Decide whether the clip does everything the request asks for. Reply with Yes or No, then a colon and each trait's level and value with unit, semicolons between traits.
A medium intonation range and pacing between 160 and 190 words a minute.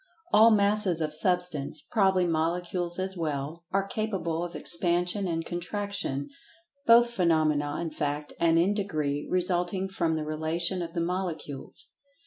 No: average, 3.2 semitones; slow, 135 wpm